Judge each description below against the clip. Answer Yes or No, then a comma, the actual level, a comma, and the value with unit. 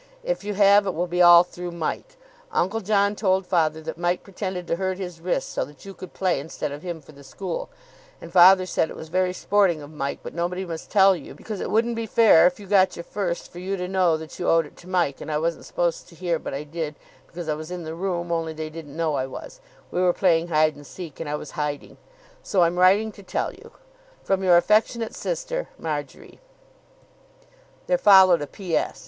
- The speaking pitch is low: No, medium, 175 Hz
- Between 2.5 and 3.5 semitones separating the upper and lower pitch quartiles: Yes, average, 3.0 semitones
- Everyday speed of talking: No, fast, 230 wpm